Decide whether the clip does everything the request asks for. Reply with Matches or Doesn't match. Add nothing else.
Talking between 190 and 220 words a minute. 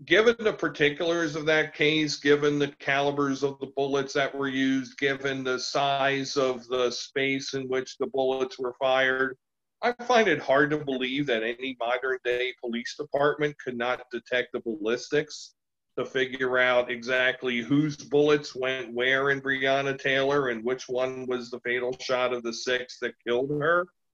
Doesn't match